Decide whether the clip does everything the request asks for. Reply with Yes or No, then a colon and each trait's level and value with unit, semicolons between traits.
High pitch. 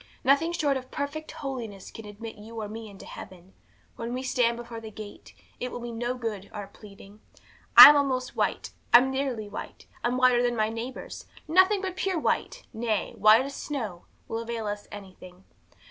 Yes: high, 235 Hz